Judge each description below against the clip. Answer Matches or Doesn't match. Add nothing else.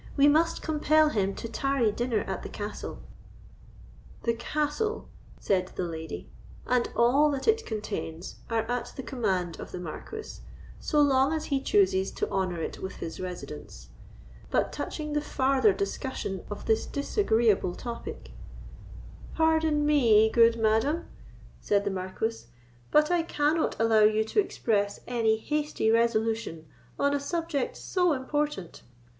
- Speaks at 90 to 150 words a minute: Matches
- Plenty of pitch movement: Matches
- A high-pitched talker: Matches